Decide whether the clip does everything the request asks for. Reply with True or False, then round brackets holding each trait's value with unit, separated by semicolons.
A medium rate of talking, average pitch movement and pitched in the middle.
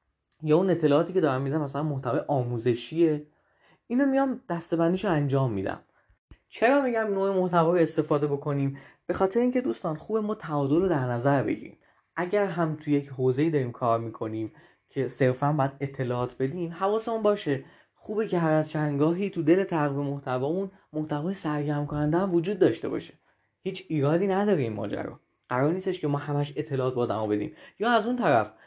False (170 wpm; 4.9 semitones; 155 Hz)